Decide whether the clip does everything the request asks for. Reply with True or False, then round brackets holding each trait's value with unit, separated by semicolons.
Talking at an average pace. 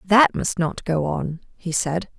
True (190 wpm)